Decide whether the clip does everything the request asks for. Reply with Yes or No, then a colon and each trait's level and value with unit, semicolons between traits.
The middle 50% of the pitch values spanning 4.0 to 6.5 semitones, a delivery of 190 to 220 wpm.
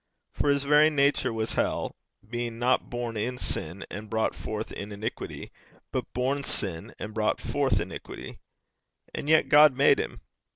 No: average, 4.6 semitones; average, 160 wpm